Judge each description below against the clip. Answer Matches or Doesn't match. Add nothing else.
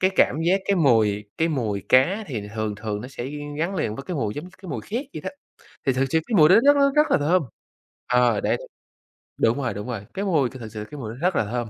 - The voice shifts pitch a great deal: Matches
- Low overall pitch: Matches